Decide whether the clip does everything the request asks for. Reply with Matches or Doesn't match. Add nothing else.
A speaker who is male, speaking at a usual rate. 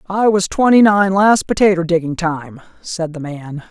Doesn't match